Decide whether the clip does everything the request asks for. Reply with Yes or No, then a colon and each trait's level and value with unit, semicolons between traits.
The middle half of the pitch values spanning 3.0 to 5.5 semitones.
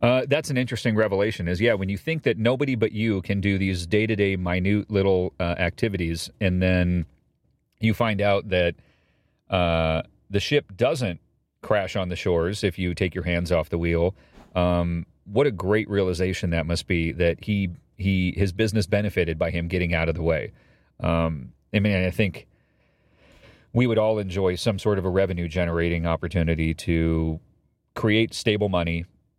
Yes: average, 3.6 semitones